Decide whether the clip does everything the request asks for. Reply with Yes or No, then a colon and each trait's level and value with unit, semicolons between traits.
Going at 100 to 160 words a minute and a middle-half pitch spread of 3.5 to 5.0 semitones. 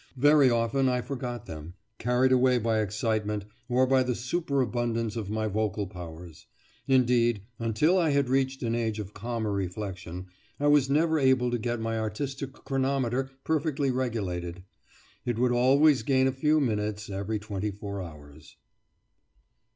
Yes: average, 150 wpm; average, 4.0 semitones